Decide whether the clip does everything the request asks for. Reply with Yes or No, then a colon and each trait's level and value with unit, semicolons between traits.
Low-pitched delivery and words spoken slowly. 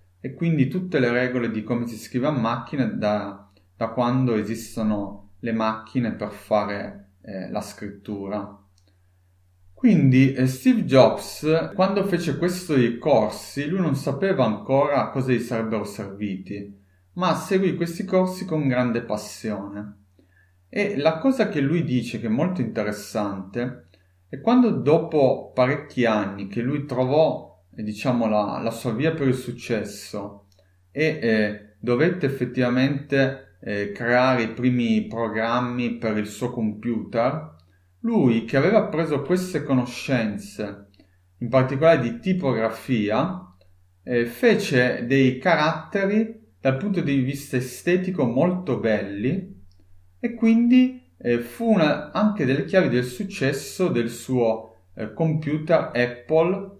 No: low, 125 Hz; average, 130 wpm